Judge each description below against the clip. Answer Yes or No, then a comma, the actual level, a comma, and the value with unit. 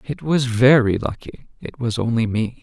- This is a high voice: No, low, 120 Hz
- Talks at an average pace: Yes, average, 185 wpm